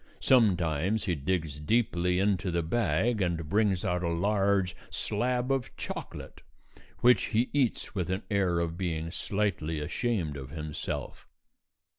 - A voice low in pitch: Yes, very low, 90 Hz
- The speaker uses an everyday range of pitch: Yes, average, 4.5 semitones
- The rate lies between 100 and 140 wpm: Yes, slow, 135 wpm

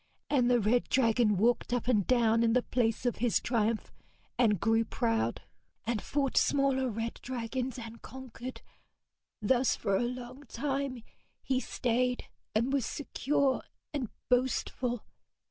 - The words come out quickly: No, average, 140 wpm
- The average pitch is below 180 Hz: No, high, 245 Hz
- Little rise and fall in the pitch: Yes, narrow, 2.3 semitones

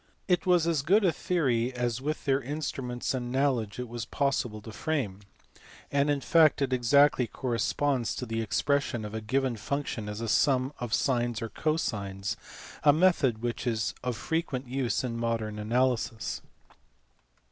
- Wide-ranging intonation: No, average, 3.8 semitones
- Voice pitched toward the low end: Yes, low, 125 Hz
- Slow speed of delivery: No, average, 160 wpm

